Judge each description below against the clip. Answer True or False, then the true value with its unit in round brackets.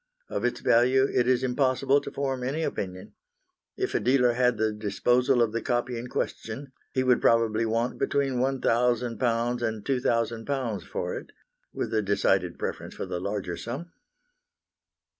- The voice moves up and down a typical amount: False (2.3 semitones)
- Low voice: True (120 Hz)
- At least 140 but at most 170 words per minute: True (155 wpm)